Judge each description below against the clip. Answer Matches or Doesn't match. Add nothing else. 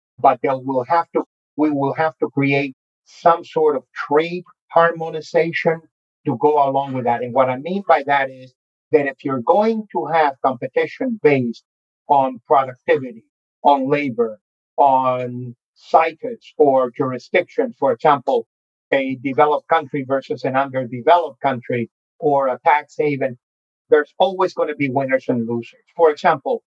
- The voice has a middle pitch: Matches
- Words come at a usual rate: Matches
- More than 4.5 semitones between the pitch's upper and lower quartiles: Doesn't match